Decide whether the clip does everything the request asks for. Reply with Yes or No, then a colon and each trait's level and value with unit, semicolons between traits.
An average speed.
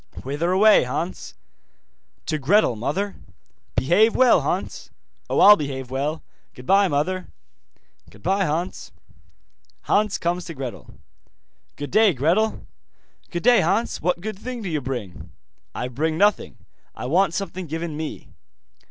No: slow, 130 wpm